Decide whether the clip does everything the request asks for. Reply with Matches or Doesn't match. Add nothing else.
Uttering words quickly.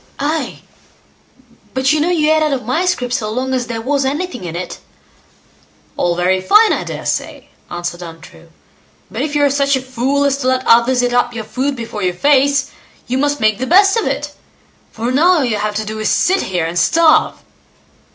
Matches